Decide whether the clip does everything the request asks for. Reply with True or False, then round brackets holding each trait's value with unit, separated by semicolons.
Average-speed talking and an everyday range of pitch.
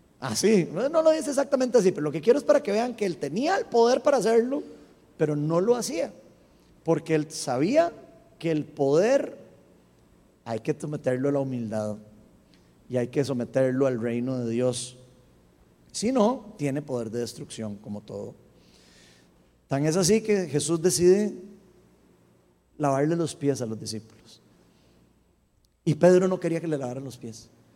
False (160 wpm; 8.5 semitones)